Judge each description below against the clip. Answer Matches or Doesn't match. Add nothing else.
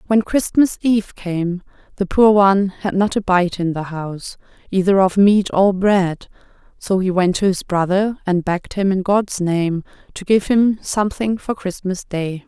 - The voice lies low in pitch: Doesn't match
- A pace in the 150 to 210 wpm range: Matches